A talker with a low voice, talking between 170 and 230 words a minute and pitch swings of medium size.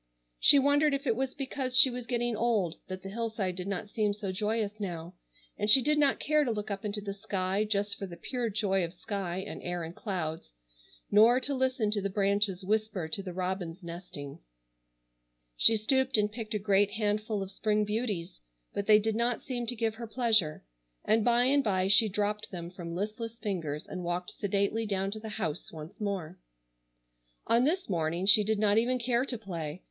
No: high, 210 Hz; average, 200 wpm; average, 3.6 semitones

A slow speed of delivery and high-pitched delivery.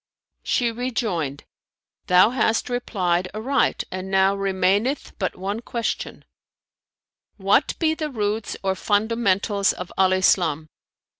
Yes: slow, 115 wpm; high, 200 Hz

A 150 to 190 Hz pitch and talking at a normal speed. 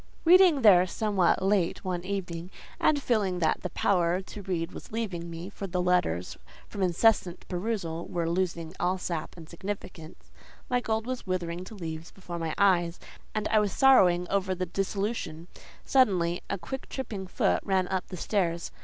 Yes: medium, 185 Hz; average, 160 wpm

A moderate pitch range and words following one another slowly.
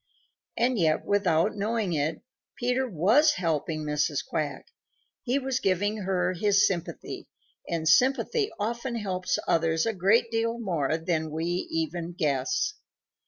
No: wide, 5.9 semitones; slow, 130 wpm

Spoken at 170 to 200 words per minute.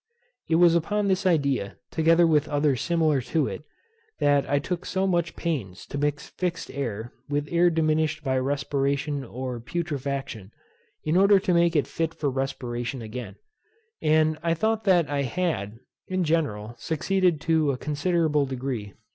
No: average, 160 wpm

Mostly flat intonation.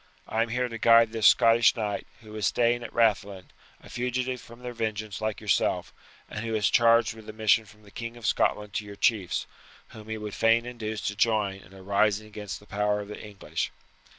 Yes: narrow, 1.9 semitones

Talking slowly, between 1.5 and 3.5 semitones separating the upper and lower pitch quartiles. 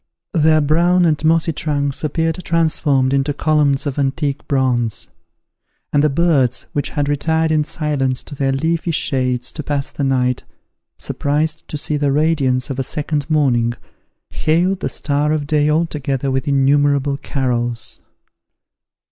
No: average, 150 wpm; narrow, 2.5 semitones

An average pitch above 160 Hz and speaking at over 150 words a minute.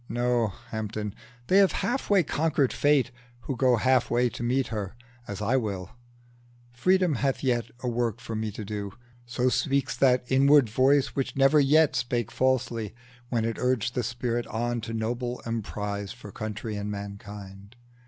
No: low, 120 Hz; average, 165 wpm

